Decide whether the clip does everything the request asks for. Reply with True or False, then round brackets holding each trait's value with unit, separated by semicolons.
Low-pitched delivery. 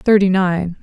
False (185 Hz)